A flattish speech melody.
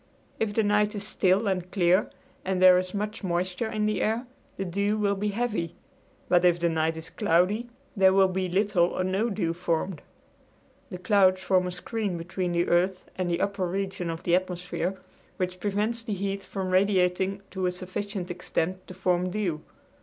Yes: narrow, 2.2 semitones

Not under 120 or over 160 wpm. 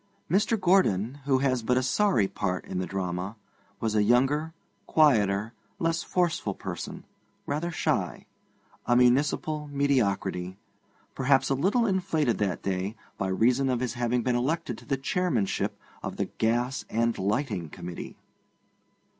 Yes: average, 140 wpm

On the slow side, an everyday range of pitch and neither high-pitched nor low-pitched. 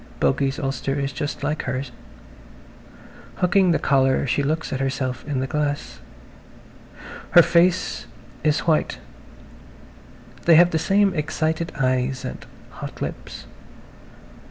Yes: slow, 120 wpm; average, 3.4 semitones; medium, 145 Hz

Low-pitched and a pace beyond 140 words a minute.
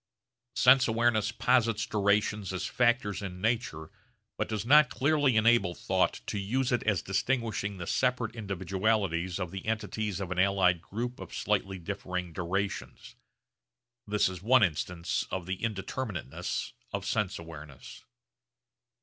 No: low, 100 Hz; slow, 135 wpm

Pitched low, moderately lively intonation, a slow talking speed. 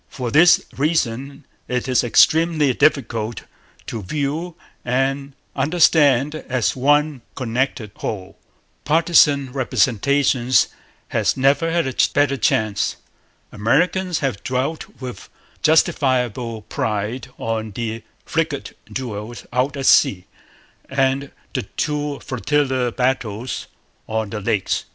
Yes: low, 130 Hz; average, 4.0 semitones; slow, 105 wpm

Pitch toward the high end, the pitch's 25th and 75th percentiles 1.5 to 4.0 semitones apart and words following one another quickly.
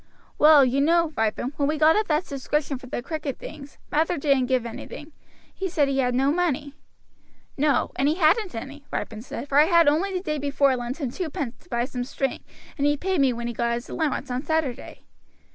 Yes: very high, 285 Hz; average, 3.5 semitones; fast, 215 wpm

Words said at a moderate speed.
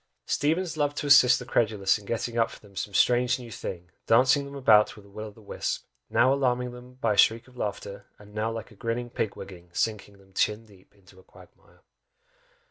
No: fast, 215 wpm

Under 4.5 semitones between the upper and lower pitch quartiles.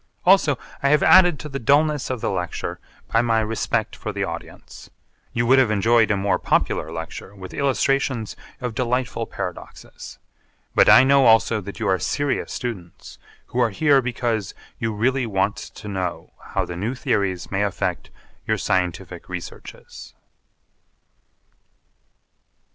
No: average, 4.9 semitones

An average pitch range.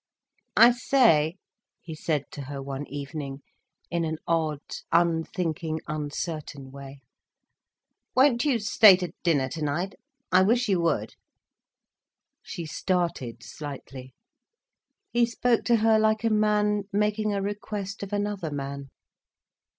No: wide, 6.3 semitones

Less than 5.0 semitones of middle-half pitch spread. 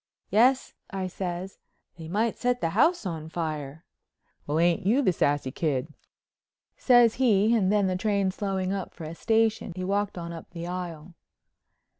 Yes: average, 4.1 semitones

